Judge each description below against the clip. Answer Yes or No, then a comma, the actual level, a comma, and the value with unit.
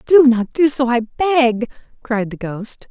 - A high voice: Yes, very high, 250 Hz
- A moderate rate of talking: Yes, average, 185 wpm